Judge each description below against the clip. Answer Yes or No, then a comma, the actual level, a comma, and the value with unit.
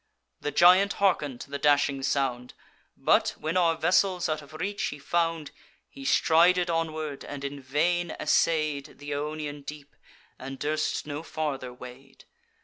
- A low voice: No, medium, 150 Hz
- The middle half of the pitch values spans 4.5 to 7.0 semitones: No, average, 2.9 semitones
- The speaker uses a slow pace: No, average, 145 wpm